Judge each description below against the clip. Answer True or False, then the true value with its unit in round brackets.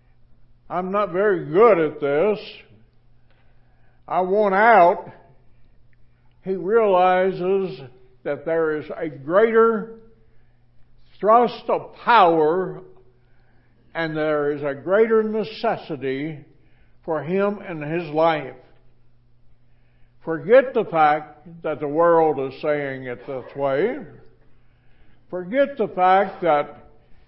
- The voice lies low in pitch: False (155 Hz)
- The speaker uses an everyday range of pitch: False (7.5 semitones)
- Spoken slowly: True (100 wpm)